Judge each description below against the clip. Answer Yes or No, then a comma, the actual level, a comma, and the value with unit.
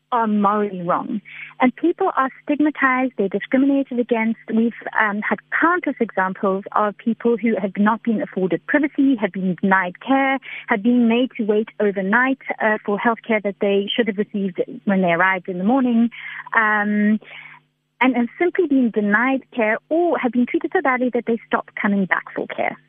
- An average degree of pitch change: Yes, average, 4.0 semitones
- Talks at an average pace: Yes, average, 180 wpm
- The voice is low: No, high, 230 Hz